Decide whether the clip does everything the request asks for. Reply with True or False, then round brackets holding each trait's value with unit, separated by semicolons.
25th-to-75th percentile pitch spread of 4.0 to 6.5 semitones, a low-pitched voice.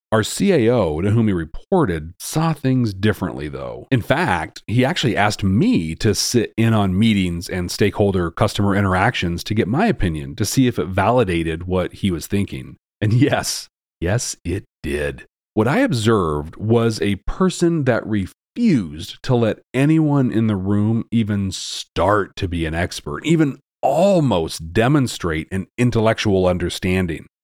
True (4.7 semitones; 100 Hz)